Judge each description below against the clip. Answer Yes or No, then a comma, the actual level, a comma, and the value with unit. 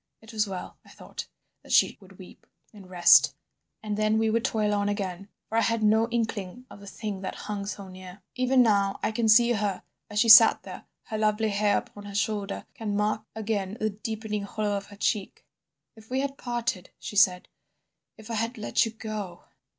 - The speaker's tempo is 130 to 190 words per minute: No, fast, 205 wpm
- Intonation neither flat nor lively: No, narrow, 1.8 semitones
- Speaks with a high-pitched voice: Yes, high, 215 Hz